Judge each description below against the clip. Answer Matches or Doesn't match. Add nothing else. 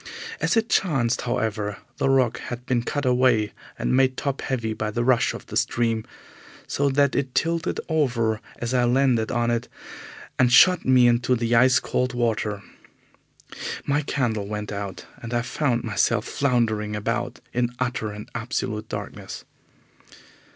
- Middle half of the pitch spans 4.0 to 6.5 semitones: Doesn't match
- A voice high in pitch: Doesn't match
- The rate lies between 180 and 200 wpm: Doesn't match